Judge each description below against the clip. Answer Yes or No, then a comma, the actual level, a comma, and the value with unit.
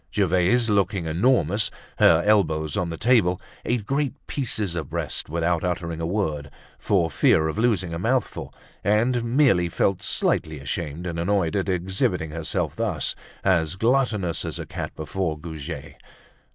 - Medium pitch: No, very low, 90 Hz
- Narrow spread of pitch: No, average, 4.4 semitones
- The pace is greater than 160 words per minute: No, average, 150 wpm